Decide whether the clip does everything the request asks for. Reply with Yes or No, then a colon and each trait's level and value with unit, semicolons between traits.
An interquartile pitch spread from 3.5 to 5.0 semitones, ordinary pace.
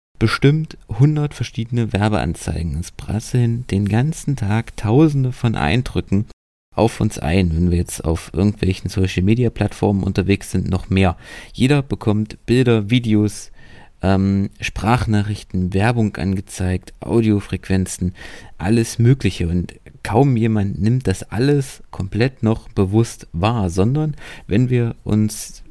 No: average, 3.9 semitones; slow, 120 wpm